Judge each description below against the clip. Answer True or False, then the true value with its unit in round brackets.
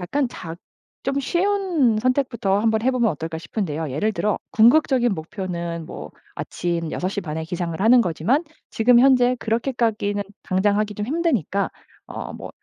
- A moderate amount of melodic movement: False (6.2 semitones)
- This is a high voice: True (215 Hz)